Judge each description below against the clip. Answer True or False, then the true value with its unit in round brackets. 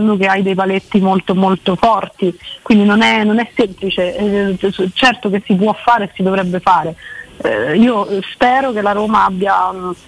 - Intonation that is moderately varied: False (2.3 semitones)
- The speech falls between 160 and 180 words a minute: True (165 wpm)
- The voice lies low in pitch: False (200 Hz)